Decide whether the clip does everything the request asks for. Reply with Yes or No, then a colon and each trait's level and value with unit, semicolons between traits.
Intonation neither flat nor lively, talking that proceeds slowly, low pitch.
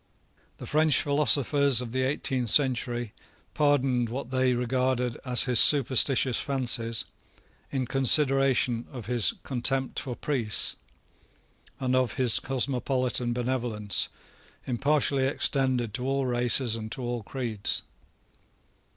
No: narrow, 2.1 semitones; slow, 115 wpm; low, 130 Hz